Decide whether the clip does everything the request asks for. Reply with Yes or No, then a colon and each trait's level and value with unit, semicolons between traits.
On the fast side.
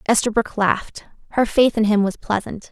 No: average, 175 wpm